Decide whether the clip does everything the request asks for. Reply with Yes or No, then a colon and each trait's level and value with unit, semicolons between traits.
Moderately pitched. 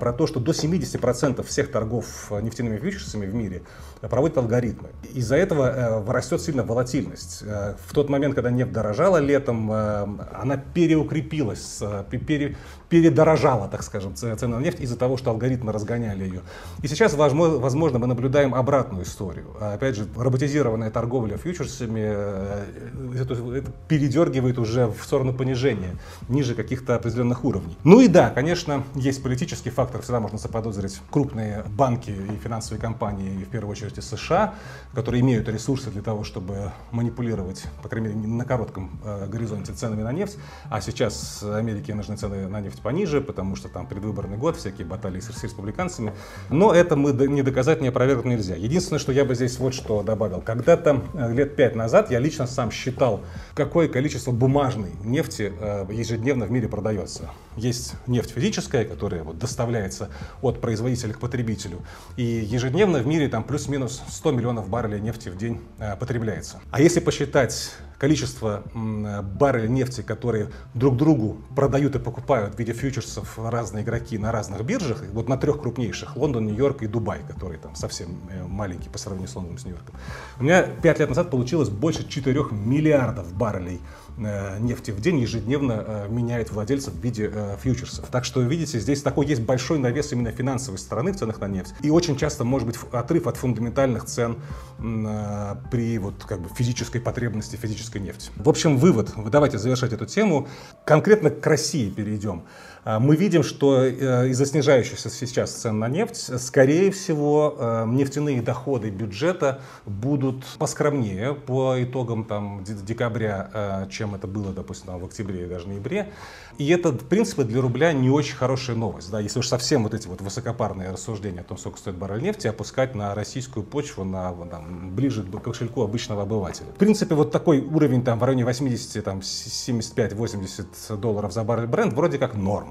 No: low, 120 Hz